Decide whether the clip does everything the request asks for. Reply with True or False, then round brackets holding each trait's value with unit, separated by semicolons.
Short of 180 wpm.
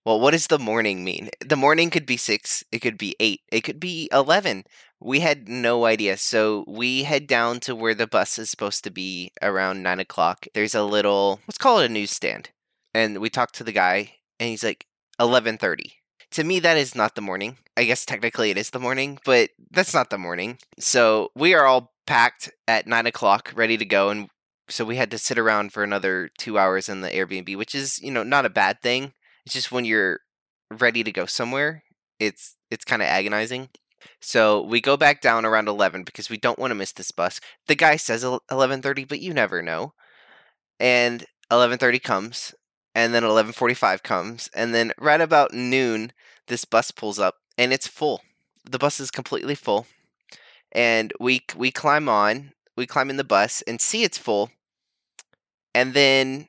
False (195 wpm)